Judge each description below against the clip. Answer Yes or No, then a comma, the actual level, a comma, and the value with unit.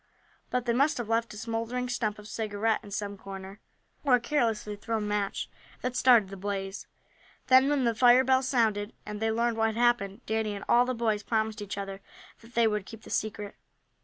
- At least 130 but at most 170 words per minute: No, fast, 205 wpm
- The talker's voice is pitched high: Yes, high, 220 Hz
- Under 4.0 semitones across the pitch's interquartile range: Yes, narrow, 2.6 semitones